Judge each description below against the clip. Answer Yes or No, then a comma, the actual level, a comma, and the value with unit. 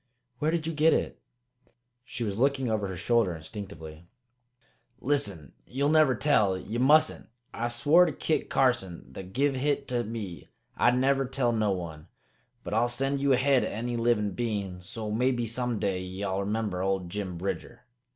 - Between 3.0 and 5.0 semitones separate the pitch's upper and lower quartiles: No, wide, 5.5 semitones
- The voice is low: Yes, low, 115 Hz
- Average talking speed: Yes, average, 170 wpm